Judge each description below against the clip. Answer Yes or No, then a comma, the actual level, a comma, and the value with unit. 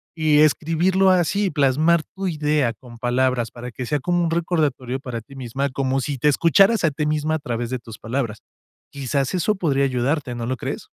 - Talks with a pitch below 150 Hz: Yes, medium, 140 Hz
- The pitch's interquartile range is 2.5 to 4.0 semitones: No, average, 4.4 semitones